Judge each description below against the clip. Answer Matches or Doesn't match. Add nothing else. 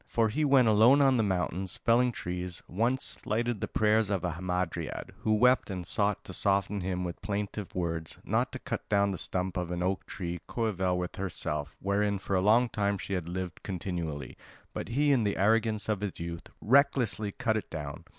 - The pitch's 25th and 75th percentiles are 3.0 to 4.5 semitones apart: Matches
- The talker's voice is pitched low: Matches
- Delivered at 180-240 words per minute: Matches